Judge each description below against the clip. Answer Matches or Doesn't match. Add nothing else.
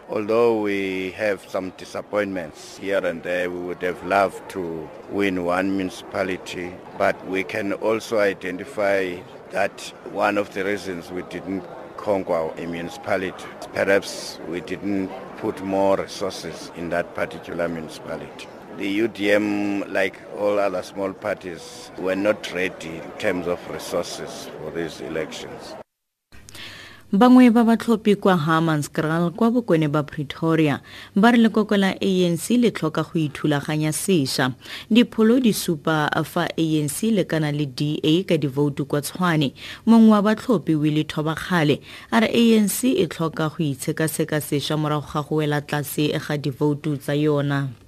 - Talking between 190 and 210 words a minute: Doesn't match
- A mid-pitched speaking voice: Matches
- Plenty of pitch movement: Matches